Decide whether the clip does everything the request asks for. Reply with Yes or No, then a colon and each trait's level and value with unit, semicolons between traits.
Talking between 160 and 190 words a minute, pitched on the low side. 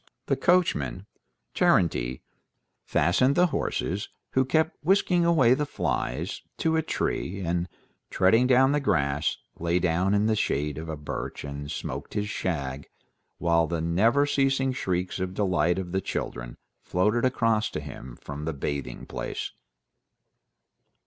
No: average, 140 wpm; very low, 95 Hz